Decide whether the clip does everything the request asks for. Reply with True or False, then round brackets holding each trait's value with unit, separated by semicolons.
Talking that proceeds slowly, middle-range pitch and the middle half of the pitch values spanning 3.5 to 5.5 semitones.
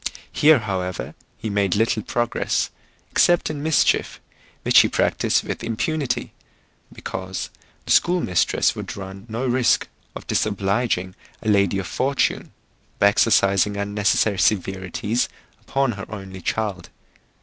False (125 wpm; 105 Hz; 3.8 semitones)